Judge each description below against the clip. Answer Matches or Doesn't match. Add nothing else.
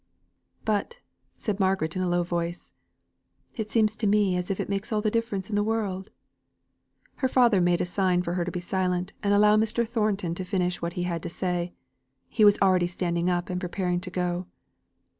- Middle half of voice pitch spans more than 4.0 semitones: Doesn't match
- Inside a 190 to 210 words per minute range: Matches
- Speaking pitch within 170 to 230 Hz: Matches